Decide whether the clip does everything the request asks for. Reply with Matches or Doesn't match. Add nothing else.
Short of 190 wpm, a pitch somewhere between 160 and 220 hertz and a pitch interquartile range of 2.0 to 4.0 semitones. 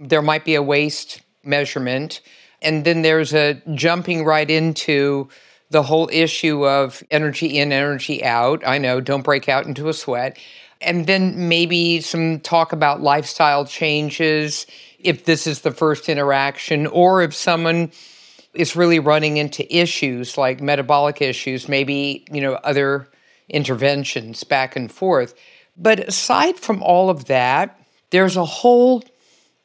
Doesn't match